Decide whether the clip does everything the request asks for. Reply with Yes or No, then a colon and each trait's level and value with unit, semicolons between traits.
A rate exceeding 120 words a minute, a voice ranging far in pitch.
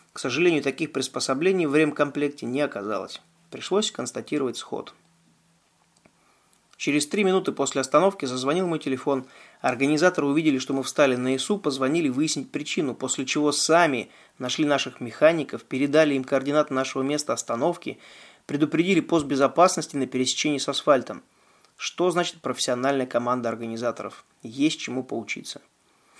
No: average, 130 wpm; average, 3.2 semitones